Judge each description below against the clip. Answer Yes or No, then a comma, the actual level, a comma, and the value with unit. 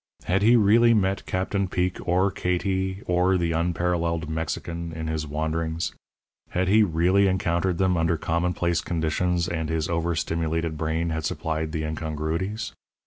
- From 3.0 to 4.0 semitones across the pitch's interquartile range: No, narrow, 2.5 semitones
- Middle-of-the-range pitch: No, very low, 85 Hz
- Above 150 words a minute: No, average, 145 wpm